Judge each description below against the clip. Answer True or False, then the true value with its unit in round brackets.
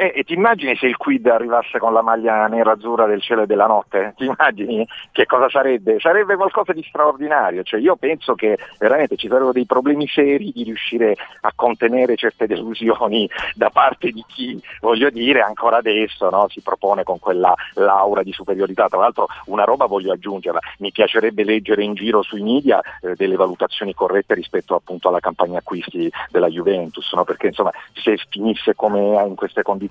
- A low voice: True (120 Hz)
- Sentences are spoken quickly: True (185 wpm)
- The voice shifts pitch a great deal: True (6.0 semitones)